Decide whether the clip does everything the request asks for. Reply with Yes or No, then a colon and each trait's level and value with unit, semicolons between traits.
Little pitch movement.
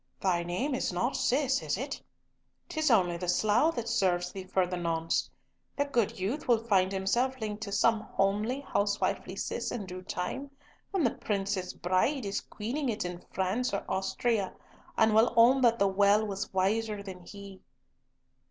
No: average, 4.1 semitones